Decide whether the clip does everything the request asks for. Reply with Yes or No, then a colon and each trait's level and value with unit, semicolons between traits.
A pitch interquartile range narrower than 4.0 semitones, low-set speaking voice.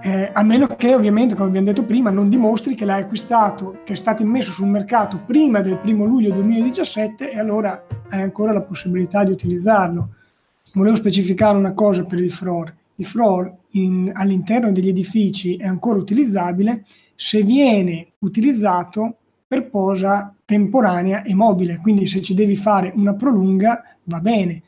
No: narrow, 2.6 semitones; high, 205 Hz